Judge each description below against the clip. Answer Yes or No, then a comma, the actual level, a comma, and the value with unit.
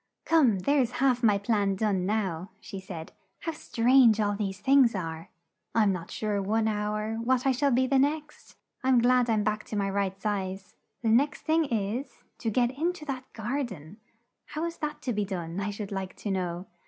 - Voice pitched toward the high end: Yes, high, 220 Hz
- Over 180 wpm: Yes, average, 200 wpm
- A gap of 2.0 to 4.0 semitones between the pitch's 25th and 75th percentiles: No, average, 4.7 semitones